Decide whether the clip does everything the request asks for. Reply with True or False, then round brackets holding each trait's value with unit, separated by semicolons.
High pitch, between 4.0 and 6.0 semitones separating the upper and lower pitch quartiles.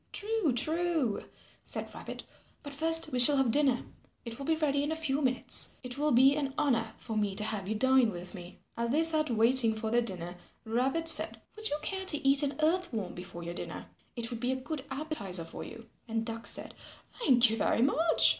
True (260 Hz; 5.1 semitones)